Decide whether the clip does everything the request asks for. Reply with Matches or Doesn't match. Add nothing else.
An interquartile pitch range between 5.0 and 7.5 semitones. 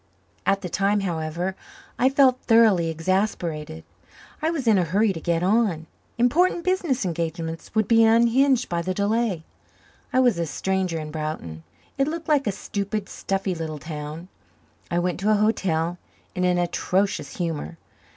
Matches